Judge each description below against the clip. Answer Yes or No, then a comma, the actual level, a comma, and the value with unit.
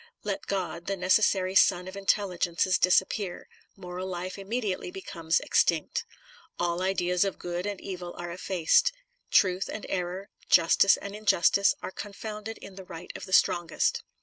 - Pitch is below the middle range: No, medium, 185 Hz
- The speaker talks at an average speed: Yes, average, 150 wpm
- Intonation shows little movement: Yes, narrow, 2.0 semitones